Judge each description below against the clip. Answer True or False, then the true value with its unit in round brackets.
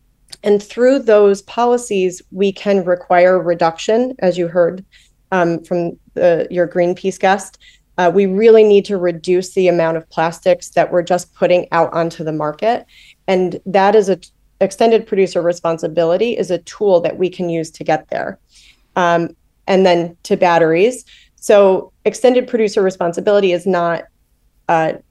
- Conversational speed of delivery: True (155 wpm)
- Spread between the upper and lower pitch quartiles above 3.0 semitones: False (2.7 semitones)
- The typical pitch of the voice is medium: True (180 Hz)